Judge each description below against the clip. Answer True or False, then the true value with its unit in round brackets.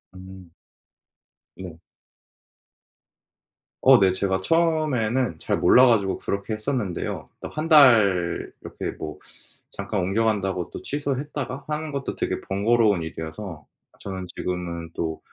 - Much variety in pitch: True (6.1 semitones)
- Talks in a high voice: False (100 Hz)